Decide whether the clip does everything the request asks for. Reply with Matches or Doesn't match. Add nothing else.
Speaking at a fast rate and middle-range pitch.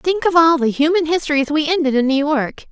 Doesn't match